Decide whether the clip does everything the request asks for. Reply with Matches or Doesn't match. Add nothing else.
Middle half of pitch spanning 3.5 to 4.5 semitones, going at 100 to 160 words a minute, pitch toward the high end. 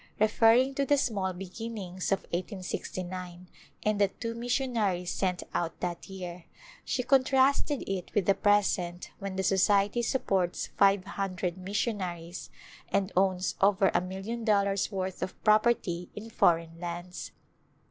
Doesn't match